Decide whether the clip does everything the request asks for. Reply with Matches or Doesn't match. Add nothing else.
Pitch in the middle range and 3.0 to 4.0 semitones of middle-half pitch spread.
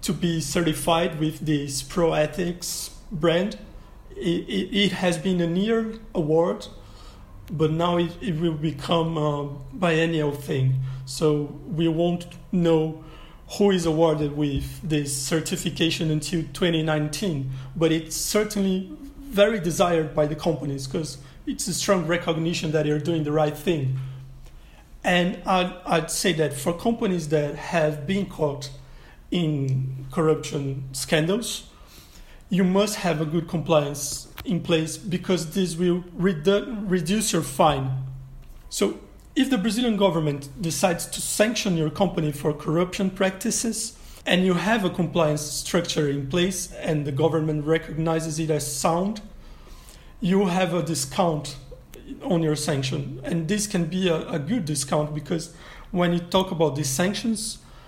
Matches